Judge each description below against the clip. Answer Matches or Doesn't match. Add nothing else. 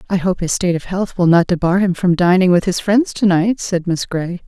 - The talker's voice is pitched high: Doesn't match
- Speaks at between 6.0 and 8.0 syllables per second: Doesn't match